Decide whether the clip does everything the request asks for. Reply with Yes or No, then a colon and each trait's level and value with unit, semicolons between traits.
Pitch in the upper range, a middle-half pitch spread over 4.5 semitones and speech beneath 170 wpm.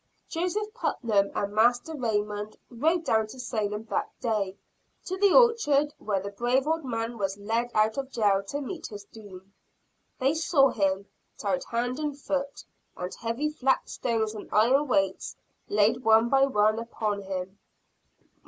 Yes: high, 230 Hz; average, 5.1 semitones; average, 155 wpm